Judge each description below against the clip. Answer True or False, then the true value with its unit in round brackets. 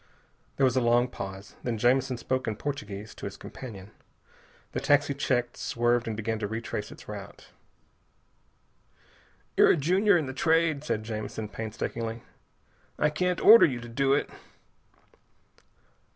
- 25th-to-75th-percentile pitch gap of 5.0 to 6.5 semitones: False (4.1 semitones)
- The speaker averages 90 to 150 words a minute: True (145 wpm)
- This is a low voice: True (120 Hz)